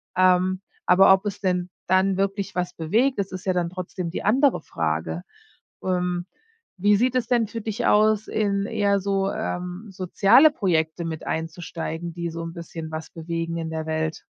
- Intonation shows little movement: No, average, 3.2 semitones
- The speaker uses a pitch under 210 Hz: Yes, medium, 185 Hz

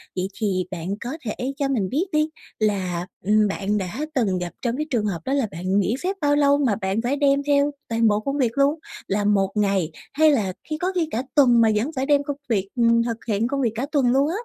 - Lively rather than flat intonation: Yes, wide, 5.8 semitones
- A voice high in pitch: Yes, high, 230 Hz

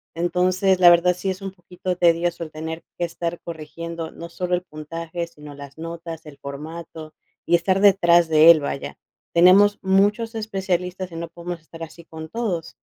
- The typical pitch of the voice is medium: Yes, medium, 170 Hz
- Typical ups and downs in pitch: No, narrow, 2.0 semitones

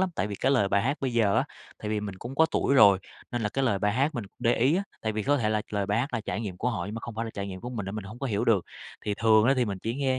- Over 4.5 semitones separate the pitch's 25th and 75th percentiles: No, average, 3.6 semitones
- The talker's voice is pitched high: No, low, 110 Hz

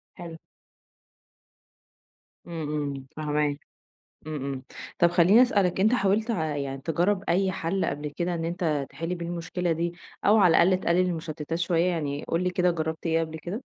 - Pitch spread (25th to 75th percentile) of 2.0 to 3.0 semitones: Yes, narrow, 2.6 semitones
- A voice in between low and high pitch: Yes, medium, 170 Hz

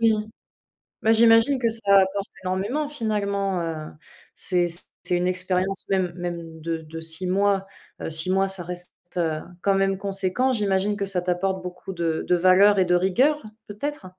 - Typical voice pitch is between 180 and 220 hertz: Yes, high, 190 Hz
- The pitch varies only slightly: Yes, narrow, 2.3 semitones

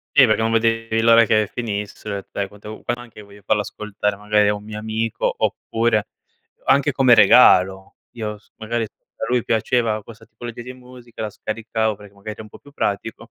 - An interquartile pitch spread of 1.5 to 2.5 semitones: Yes, narrow, 1.9 semitones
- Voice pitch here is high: No, low, 110 Hz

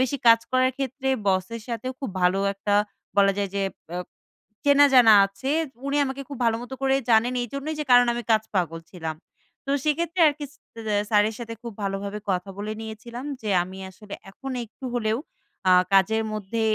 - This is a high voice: Yes, high, 225 Hz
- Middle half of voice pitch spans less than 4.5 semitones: No, average, 4.8 semitones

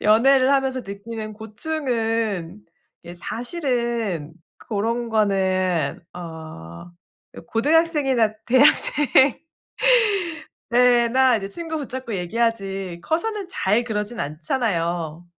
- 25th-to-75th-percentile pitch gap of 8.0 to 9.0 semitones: No, wide, 5.5 semitones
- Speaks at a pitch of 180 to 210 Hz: No, high, 225 Hz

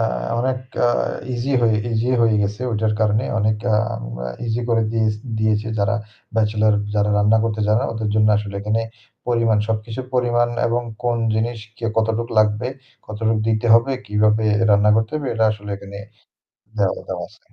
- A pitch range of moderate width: No, narrow, 1.5 semitones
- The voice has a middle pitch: No, low, 110 Hz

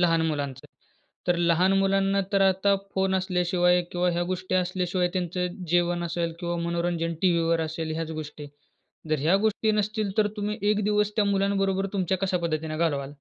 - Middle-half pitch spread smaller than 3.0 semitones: Yes, narrow, 2.6 semitones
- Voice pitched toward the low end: No, medium, 180 Hz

